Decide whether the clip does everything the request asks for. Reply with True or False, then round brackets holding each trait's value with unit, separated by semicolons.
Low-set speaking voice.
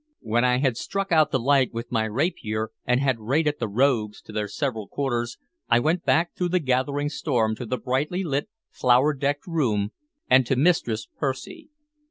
True (130 Hz)